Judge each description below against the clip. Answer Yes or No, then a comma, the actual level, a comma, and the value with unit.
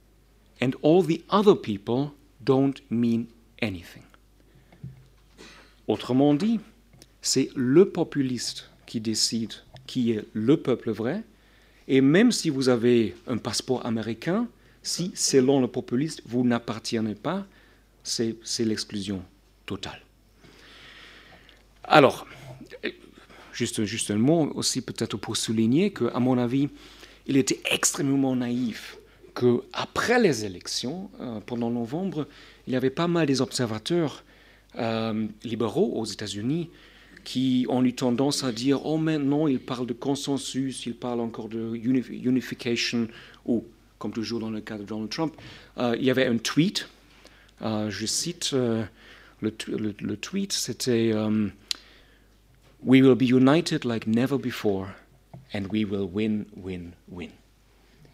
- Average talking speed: No, slow, 130 wpm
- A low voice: Yes, low, 120 Hz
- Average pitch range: Yes, average, 3.4 semitones